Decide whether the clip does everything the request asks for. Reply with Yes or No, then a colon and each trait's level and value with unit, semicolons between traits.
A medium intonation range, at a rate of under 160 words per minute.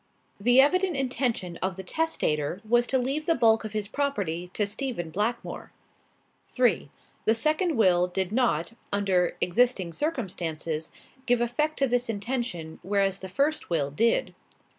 No: wide, 6.3 semitones; average, 145 wpm